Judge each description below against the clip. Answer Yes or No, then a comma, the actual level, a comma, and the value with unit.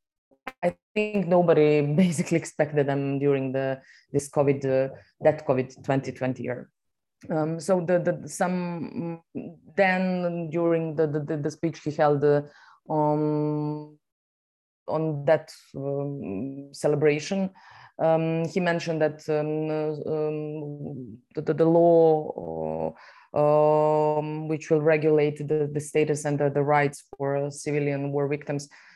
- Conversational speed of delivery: No, slow, 120 wpm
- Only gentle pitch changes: Yes, narrow, 2.2 semitones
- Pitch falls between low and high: Yes, medium, 150 Hz